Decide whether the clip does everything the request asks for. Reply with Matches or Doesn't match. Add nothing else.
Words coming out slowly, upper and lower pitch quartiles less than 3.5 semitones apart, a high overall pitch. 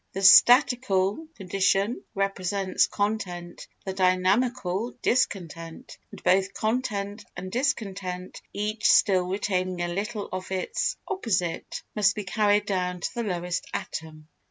Matches